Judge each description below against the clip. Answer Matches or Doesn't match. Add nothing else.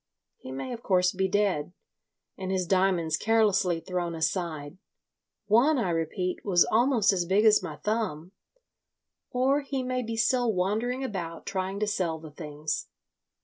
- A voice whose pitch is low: Doesn't match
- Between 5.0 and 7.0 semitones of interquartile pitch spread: Doesn't match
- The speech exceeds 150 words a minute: Doesn't match